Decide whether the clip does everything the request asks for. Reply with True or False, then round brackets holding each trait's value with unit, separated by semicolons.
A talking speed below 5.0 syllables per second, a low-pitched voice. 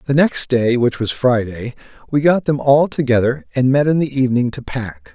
False (5.1 syllables/s; 125 Hz)